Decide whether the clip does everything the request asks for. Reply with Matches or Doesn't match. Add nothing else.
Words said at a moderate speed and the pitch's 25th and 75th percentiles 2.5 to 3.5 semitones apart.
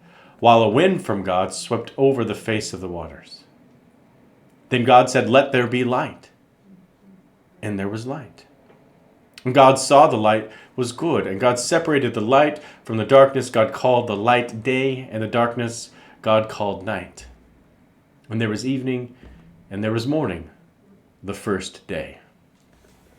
Doesn't match